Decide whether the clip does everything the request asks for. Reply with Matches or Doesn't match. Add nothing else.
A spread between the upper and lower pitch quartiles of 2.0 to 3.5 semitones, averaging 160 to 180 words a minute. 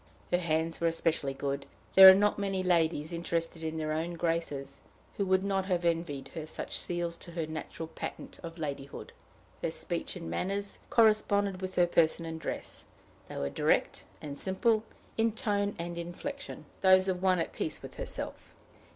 Matches